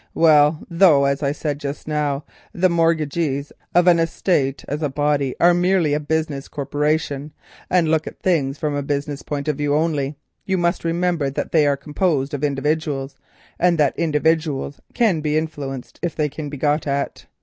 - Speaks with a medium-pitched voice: Yes, medium, 150 Hz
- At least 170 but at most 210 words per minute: Yes, average, 180 wpm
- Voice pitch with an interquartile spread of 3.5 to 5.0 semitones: No, narrow, 2.5 semitones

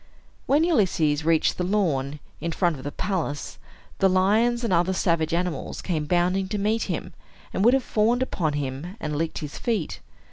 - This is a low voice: No, medium, 180 Hz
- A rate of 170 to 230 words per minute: Yes, average, 180 wpm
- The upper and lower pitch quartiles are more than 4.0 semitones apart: Yes, average, 5.1 semitones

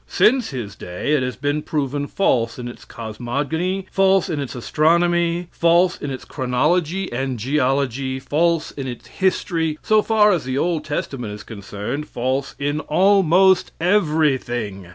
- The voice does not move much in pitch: No, average, 5.2 semitones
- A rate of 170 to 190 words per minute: No, average, 150 wpm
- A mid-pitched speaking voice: Yes, medium, 150 Hz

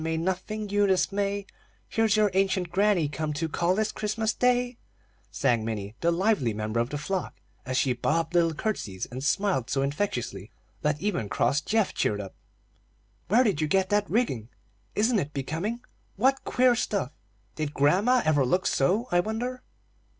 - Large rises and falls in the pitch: Yes, wide, 6.8 semitones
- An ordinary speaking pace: Yes, average, 165 wpm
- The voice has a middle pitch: Yes, medium, 180 Hz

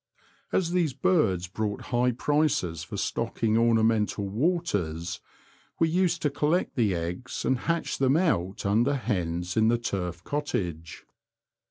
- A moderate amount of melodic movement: No, wide, 8.6 semitones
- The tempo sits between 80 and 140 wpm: Yes, slow, 135 wpm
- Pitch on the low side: Yes, low, 115 Hz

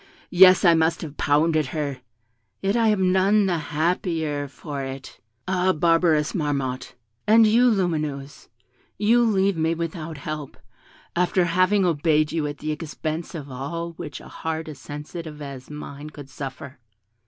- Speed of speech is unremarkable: Yes, average, 150 wpm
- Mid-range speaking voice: Yes, medium, 160 Hz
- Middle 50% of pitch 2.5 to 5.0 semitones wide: Yes, average, 3.6 semitones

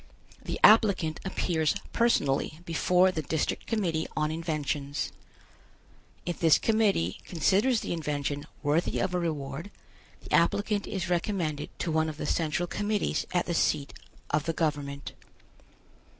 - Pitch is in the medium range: Yes, medium, 165 Hz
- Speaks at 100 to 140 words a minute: Yes, slow, 135 wpm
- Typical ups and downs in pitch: Yes, average, 3.8 semitones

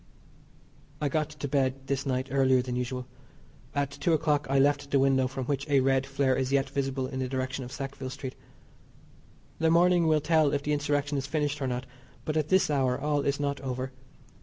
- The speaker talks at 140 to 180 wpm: No, fast, 205 wpm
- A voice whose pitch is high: No, medium, 140 Hz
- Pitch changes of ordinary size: No, narrow, 1.8 semitones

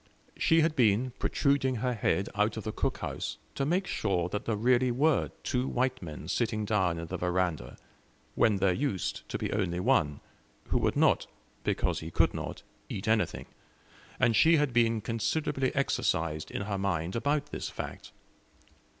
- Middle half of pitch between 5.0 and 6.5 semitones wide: Yes, wide, 5.6 semitones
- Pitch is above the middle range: No, low, 110 Hz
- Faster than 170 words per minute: No, average, 165 wpm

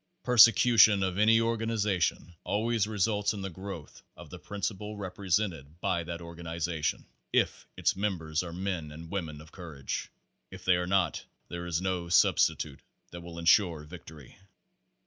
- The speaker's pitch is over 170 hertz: No, very low, 90 Hz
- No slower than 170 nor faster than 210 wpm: No, average, 150 wpm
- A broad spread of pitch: No, average, 3.6 semitones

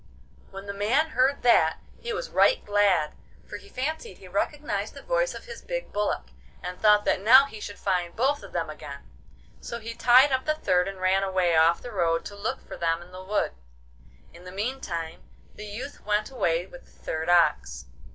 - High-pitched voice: Yes, high, 205 Hz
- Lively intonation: Yes, wide, 6.4 semitones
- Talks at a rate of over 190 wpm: Yes, average, 200 wpm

